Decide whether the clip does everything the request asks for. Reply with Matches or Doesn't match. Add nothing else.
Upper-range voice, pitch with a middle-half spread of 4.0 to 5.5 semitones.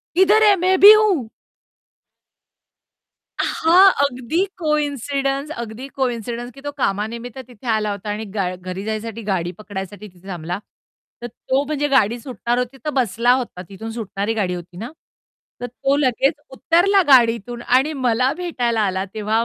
Matches